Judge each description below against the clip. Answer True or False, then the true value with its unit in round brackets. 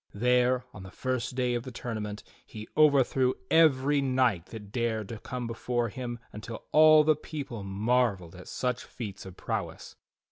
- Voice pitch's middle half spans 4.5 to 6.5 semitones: False (3.3 semitones)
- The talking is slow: False (165 wpm)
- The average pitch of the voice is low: True (120 Hz)